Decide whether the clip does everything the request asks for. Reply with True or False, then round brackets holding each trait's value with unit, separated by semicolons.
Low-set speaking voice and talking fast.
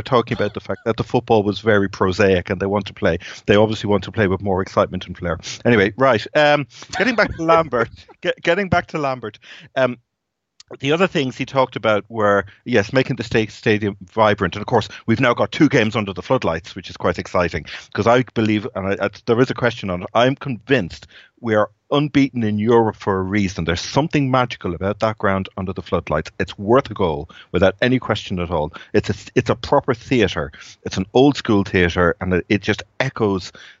True (110 Hz; 215 wpm)